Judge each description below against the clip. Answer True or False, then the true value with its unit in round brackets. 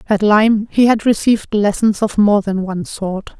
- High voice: True (210 Hz)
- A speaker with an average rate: True (195 wpm)